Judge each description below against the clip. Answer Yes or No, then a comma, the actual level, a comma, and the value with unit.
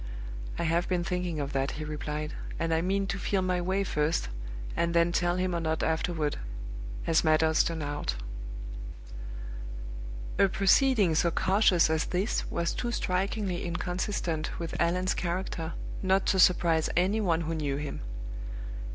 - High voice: No, medium, 170 Hz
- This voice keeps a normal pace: Yes, average, 150 wpm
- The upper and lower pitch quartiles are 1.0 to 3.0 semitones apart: Yes, average, 2.7 semitones